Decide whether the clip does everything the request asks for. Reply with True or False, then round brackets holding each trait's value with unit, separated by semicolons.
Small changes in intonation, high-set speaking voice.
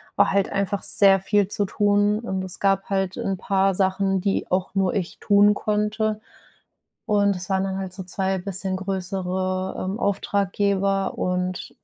True (1.2 semitones; 195 Hz)